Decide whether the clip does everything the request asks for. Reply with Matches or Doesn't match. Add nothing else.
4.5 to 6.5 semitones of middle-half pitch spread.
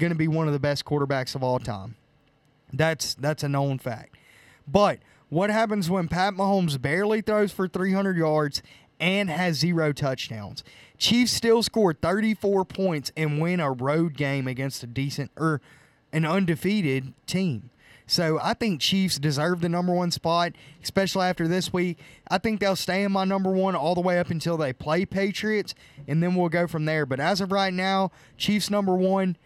Matches